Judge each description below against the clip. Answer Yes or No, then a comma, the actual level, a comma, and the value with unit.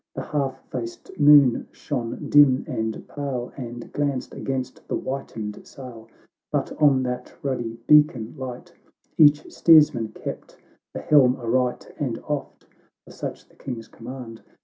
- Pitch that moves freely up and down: No, average, 3.3 semitones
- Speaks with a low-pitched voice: Yes, low, 130 Hz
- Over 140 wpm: No, slow, 135 wpm